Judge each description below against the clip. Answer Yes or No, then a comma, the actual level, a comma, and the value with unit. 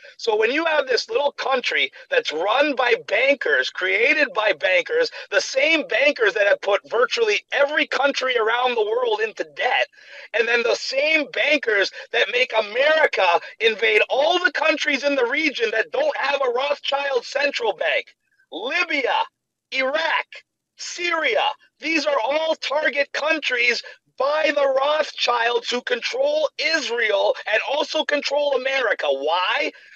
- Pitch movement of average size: No, wide, 7.0 semitones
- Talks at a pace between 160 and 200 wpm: No, average, 140 wpm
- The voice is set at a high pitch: Yes, very high, 295 Hz